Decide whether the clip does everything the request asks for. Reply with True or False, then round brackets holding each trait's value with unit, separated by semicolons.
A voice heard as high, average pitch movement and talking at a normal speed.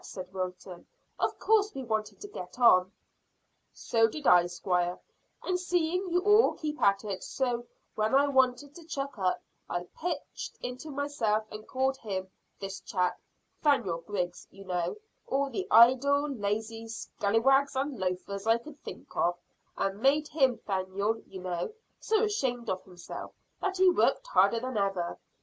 False (230 Hz; 6.9 semitones; 160 wpm)